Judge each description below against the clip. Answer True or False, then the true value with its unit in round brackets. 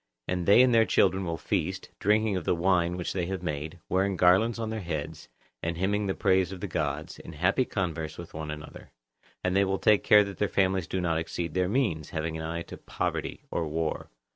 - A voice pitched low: True (90 Hz)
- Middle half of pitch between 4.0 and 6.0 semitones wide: False (3.2 semitones)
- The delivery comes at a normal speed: False (220 wpm)